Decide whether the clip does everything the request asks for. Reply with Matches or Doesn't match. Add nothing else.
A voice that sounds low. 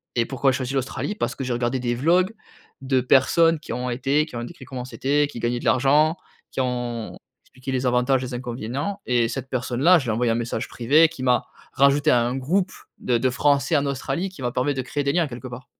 Matches